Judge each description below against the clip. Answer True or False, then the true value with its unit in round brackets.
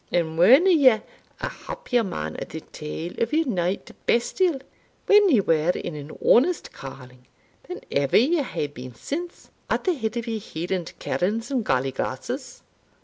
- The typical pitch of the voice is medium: False (210 Hz)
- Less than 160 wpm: False (165 wpm)